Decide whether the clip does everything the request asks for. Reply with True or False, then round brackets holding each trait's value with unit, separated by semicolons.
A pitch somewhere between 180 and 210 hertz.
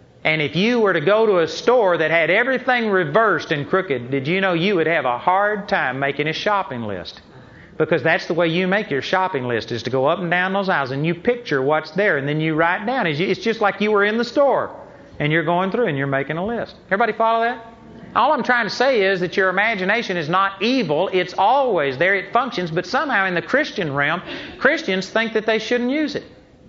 True (190 Hz)